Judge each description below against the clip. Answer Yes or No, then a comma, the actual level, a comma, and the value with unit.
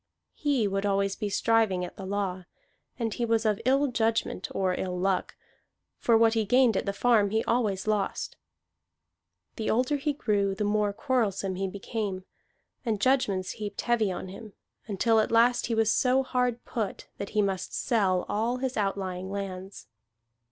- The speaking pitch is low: No, high, 210 Hz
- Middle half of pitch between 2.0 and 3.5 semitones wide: Yes, average, 3.2 semitones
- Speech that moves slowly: No, average, 170 wpm